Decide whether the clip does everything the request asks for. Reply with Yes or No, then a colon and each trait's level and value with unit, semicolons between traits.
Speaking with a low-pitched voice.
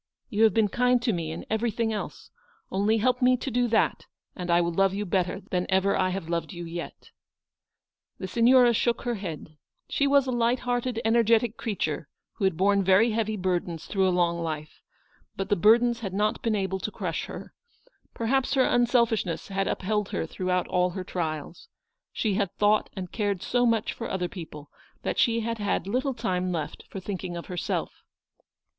No: high, 205 Hz